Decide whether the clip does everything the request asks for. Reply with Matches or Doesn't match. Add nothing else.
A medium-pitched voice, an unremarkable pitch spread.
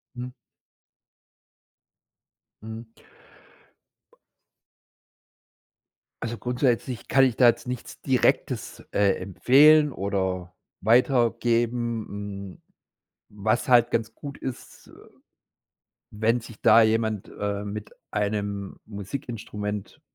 Doesn't match